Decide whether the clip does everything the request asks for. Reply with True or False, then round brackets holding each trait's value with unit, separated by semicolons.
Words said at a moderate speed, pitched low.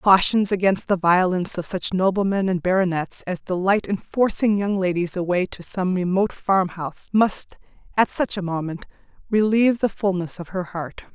False (170 wpm; 190 Hz)